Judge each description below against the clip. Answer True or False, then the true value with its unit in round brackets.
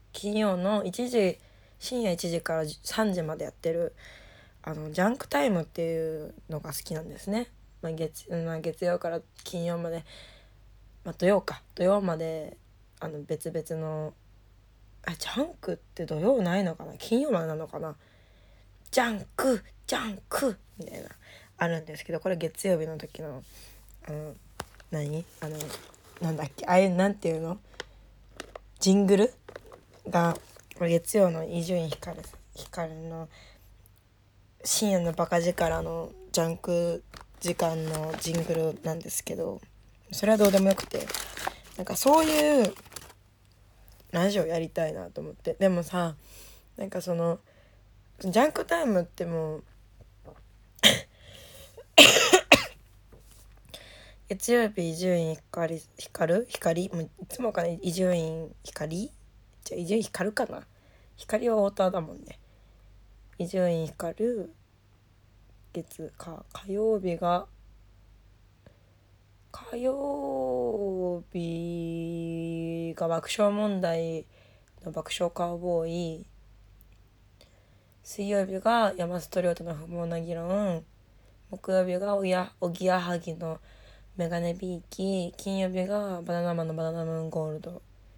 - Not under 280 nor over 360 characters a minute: False (225 characters per minute)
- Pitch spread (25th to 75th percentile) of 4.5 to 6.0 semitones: True (5.2 semitones)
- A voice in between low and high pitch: True (165 Hz)